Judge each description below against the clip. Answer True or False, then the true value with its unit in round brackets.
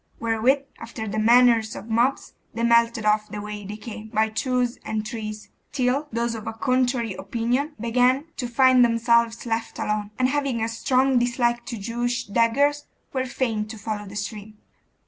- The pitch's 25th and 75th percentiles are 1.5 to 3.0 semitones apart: True (2.4 semitones)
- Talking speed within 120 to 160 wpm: False (170 wpm)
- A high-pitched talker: True (235 Hz)